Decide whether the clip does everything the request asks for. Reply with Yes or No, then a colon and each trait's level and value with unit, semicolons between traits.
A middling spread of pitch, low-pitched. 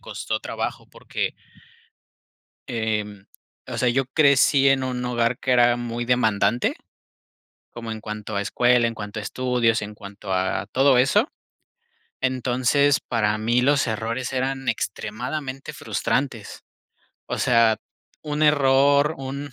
Yes: average, 3.4 semitones; low, 125 Hz